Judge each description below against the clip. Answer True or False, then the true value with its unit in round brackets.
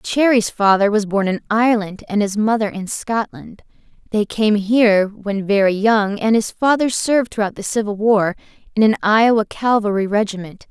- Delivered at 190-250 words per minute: False (170 wpm)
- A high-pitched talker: True (210 Hz)